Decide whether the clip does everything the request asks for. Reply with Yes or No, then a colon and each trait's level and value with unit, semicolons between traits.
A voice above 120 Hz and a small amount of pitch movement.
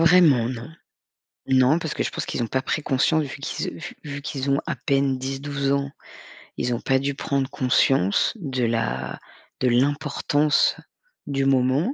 Yes: low, 135 Hz; narrow, 1.9 semitones